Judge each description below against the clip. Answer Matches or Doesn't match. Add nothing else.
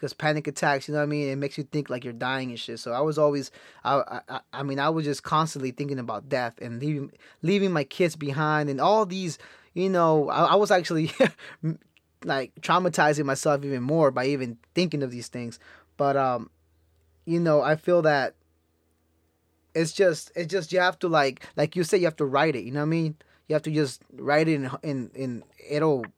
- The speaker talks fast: Matches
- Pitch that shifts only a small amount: Doesn't match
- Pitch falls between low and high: Matches